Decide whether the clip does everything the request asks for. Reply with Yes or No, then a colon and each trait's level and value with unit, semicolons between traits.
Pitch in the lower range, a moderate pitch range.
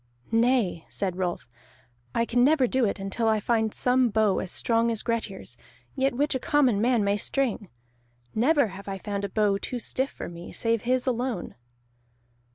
No: high, 230 Hz; average, 3.9 semitones